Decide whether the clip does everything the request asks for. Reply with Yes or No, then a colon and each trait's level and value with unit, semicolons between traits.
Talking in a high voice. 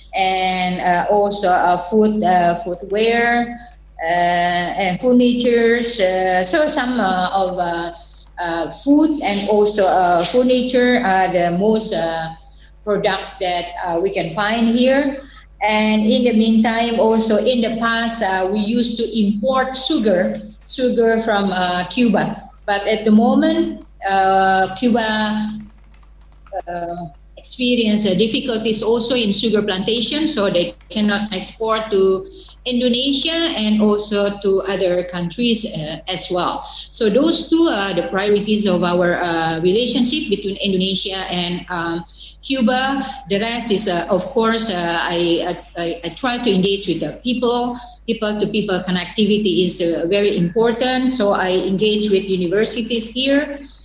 Yes: high, 205 Hz